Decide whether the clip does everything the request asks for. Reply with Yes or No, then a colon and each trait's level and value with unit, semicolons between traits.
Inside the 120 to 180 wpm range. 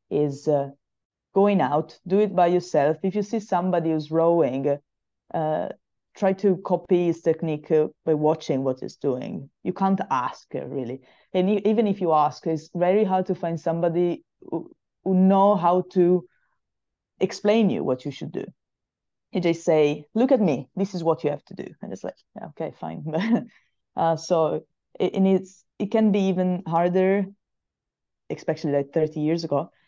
Yes: average, 170 wpm